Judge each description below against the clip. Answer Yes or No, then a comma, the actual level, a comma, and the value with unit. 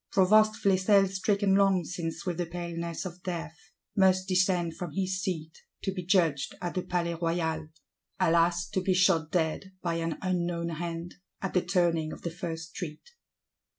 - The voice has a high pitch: No, medium, 175 Hz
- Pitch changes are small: Yes, narrow, 2.1 semitones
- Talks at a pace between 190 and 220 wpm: No, average, 160 wpm